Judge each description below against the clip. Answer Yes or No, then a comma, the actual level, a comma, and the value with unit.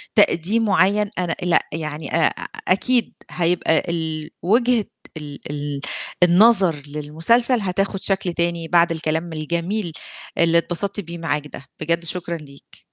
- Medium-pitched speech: Yes, medium, 170 Hz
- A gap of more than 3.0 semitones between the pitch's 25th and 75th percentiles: Yes, average, 3.6 semitones